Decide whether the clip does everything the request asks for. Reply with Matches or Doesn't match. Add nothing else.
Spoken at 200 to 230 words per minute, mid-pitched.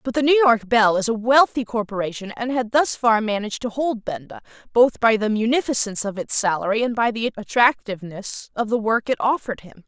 Doesn't match